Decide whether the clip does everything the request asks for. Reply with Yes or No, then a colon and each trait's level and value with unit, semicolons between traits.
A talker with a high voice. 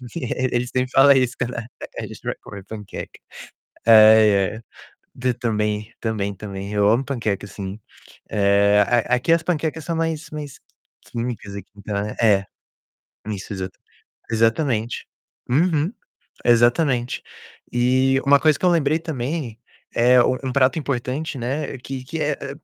No: low, 125 Hz